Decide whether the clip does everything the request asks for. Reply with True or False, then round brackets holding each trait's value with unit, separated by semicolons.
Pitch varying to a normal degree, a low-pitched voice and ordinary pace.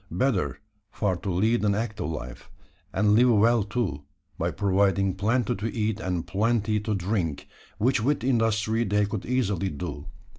True (3.1 semitones; 105 Hz; 155 wpm)